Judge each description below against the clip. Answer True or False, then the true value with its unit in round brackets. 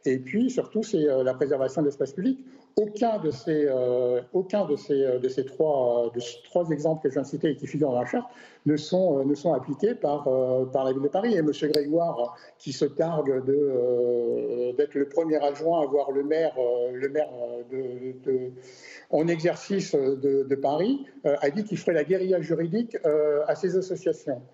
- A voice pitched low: False (145 Hz)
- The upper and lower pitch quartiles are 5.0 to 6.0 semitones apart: False (4.5 semitones)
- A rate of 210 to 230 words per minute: True (215 wpm)